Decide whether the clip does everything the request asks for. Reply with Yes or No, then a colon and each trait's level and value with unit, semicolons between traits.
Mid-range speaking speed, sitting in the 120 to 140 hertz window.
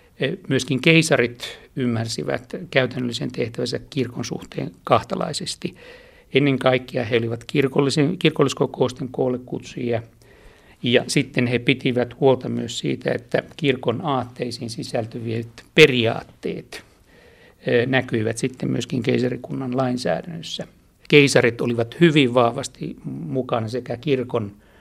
No: slow, 90 wpm; low, 125 Hz